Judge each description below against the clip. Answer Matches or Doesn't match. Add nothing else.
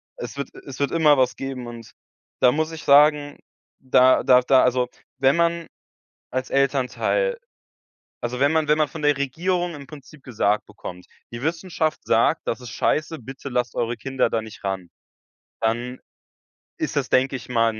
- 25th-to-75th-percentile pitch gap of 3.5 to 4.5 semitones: Matches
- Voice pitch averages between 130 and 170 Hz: Matches